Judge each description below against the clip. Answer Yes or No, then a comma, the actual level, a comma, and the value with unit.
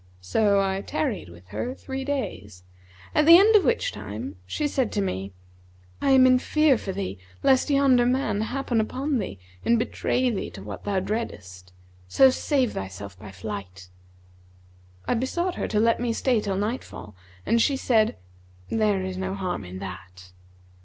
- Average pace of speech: Yes, average, 170 wpm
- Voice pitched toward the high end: Yes, high, 215 Hz